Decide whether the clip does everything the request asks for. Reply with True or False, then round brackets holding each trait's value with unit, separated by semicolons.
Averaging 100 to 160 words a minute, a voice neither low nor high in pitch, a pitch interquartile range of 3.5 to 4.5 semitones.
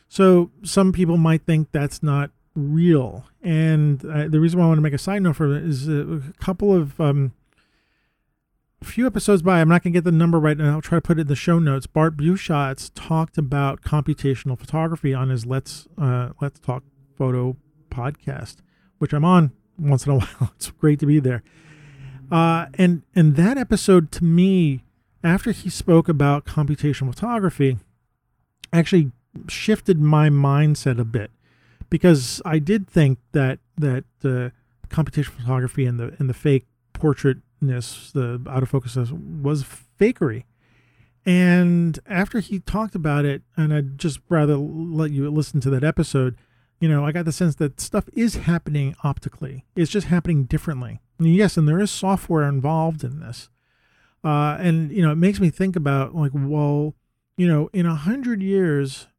False (175 wpm; 150 Hz; 3.8 semitones)